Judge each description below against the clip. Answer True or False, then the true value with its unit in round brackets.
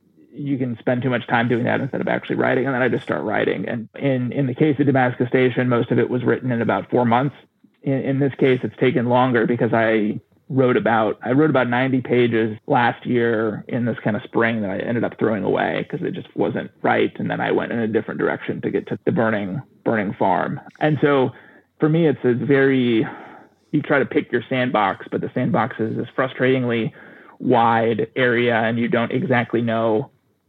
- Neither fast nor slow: False (215 wpm)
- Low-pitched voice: True (120 Hz)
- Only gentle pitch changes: True (2.2 semitones)